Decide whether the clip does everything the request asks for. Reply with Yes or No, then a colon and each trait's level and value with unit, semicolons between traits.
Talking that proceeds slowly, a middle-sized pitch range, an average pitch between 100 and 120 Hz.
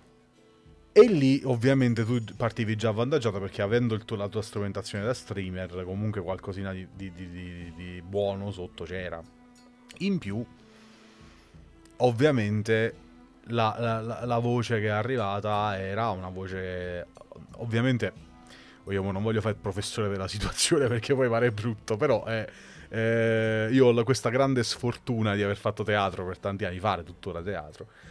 No: average, 150 wpm; average, 3.8 semitones; low, 105 Hz